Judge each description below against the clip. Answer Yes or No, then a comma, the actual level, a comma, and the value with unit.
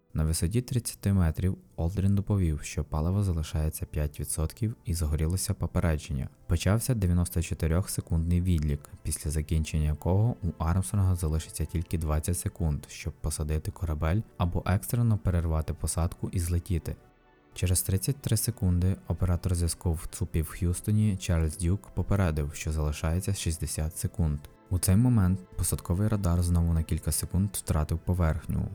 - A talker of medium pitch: No, very low, 85 Hz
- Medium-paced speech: Yes, average, 125 wpm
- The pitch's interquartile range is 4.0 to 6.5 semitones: No, average, 3.3 semitones